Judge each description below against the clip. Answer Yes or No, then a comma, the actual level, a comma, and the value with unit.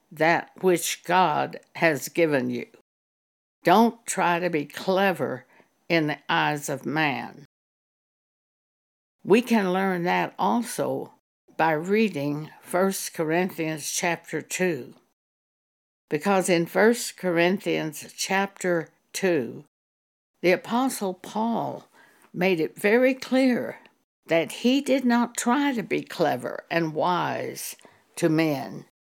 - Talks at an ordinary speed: No, slow, 105 wpm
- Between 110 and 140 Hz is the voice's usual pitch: No, medium, 175 Hz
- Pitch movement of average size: Yes, average, 4.9 semitones